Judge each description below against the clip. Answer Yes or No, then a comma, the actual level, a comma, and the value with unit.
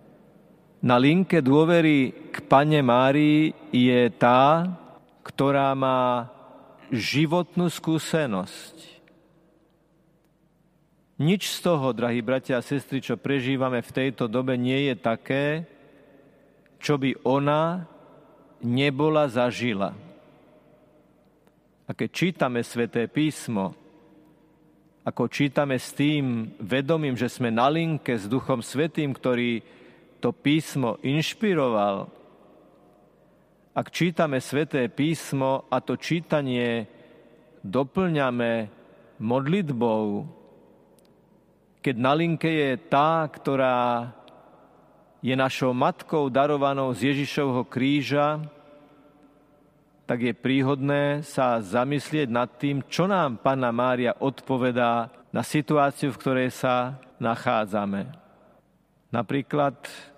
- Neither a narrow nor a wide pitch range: Yes, average, 3.9 semitones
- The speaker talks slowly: Yes, slow, 95 wpm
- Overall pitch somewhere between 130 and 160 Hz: Yes, medium, 140 Hz